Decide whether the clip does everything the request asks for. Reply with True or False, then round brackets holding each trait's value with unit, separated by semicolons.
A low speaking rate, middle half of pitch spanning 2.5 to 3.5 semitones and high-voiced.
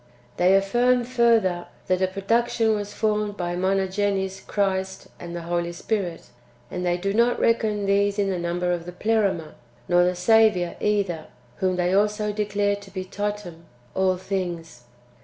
False (165 wpm; 2.8 semitones; 195 Hz)